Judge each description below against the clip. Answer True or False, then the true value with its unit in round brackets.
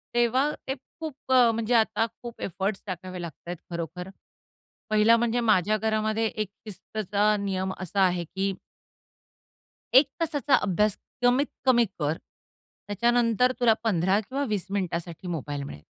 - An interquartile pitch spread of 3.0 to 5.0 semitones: True (4.2 semitones)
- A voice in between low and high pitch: False (210 Hz)